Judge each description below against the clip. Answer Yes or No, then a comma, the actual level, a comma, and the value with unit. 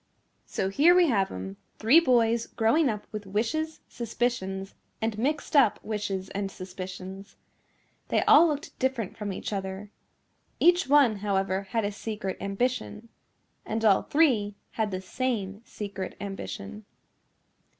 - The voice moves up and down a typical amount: Yes, average, 4.2 semitones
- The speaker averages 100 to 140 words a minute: Yes, slow, 135 wpm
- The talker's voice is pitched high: Yes, high, 210 Hz